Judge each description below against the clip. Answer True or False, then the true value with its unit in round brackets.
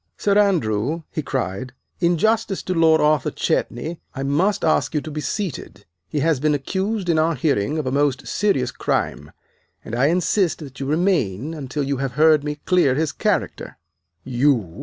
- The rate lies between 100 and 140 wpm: False (180 wpm)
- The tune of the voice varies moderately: True (4.3 semitones)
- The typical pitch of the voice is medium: True (150 Hz)